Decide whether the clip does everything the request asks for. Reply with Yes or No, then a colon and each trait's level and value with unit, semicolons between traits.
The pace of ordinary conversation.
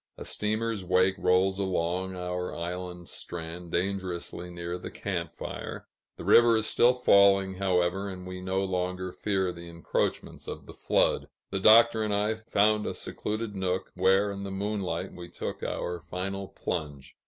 Yes: average, 160 wpm